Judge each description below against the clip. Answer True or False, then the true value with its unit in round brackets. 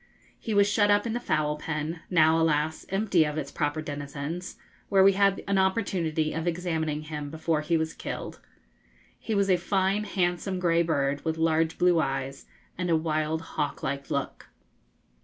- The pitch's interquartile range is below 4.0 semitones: True (3.6 semitones)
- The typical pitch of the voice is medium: True (160 Hz)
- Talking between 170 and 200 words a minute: True (175 wpm)